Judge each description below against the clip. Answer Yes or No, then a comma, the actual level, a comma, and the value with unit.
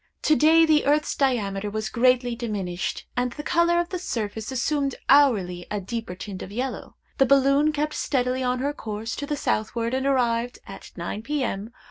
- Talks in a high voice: Yes, very high, 250 Hz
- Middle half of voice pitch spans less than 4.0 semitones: No, average, 4.8 semitones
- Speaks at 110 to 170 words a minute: No, average, 180 wpm